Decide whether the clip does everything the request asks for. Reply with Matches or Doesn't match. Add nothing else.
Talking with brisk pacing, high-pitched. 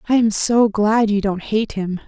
Matches